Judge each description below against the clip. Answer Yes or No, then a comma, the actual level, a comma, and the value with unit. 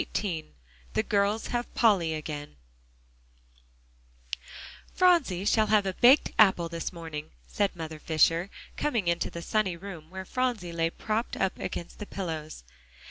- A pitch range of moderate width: Yes, average, 4.5 semitones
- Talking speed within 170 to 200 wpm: No, slow, 135 wpm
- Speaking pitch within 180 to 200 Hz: Yes, medium, 185 Hz